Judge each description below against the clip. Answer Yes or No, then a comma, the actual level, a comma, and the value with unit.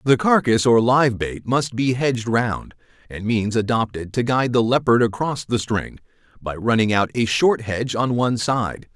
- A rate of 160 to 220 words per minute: Yes, average, 190 wpm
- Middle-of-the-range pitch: No, low, 120 Hz